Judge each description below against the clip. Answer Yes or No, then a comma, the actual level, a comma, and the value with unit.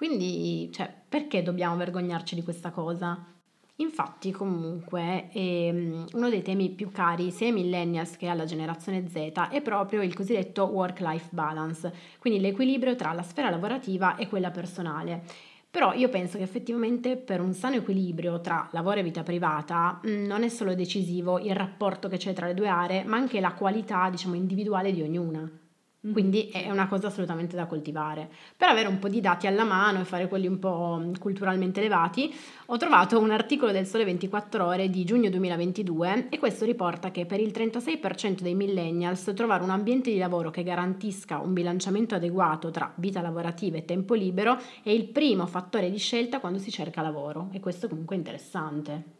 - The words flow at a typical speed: No, fast, 175 wpm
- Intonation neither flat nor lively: Yes, average, 3.1 semitones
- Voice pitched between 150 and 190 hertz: Yes, medium, 185 Hz